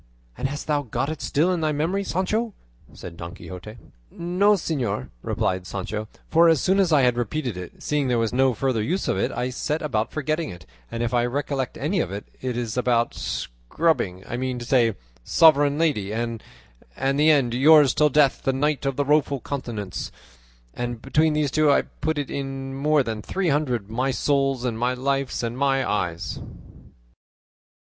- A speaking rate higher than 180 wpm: Yes, average, 190 wpm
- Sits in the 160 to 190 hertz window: No, low, 135 Hz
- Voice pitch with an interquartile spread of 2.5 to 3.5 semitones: No, average, 4.4 semitones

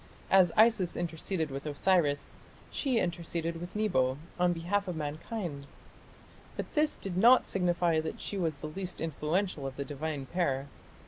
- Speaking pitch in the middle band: Yes, medium, 170 Hz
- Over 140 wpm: Yes, average, 150 wpm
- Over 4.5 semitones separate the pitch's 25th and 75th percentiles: No, average, 3.9 semitones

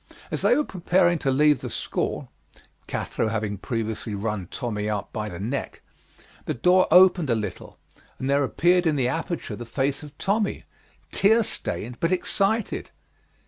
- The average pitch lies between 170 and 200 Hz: No, medium, 140 Hz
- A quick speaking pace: No, average, 160 wpm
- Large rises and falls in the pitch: Yes, wide, 8.3 semitones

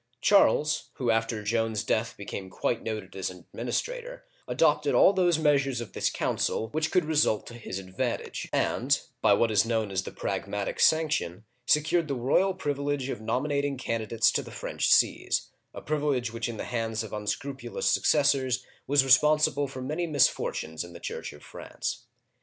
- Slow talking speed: No, average, 170 wpm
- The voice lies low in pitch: Yes, low, 125 Hz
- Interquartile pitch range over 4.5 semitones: Yes, average, 5.0 semitones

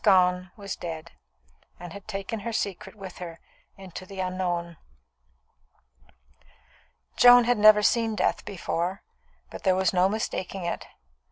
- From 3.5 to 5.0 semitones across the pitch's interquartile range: No, narrow, 2.6 semitones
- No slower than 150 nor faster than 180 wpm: No, slow, 135 wpm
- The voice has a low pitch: No, high, 190 Hz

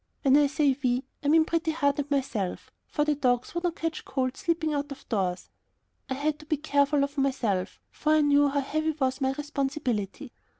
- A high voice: Yes, very high, 285 Hz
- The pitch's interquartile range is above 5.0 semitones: No, narrow, 2.5 semitones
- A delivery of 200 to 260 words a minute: Yes, fast, 205 wpm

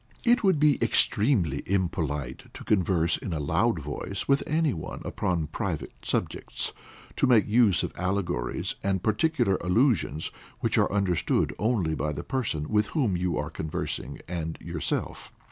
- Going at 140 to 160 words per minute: Yes, average, 150 wpm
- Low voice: Yes, very low, 95 Hz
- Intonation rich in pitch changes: Yes, wide, 6.4 semitones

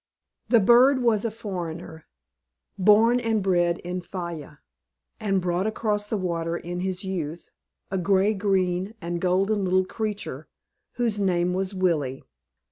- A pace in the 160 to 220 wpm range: No, slow, 135 wpm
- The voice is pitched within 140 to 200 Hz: Yes, high, 190 Hz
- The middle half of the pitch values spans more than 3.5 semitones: No, average, 3.2 semitones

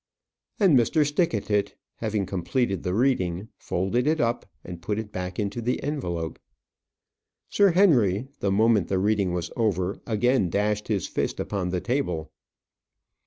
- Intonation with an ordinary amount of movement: Yes, average, 4.9 semitones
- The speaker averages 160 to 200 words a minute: No, average, 145 wpm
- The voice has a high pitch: No, low, 105 Hz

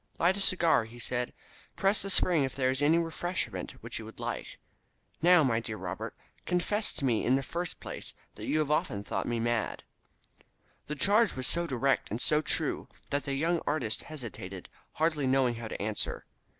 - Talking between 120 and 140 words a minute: No, average, 190 wpm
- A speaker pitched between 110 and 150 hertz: Yes, medium, 140 Hz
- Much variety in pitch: Yes, wide, 5.9 semitones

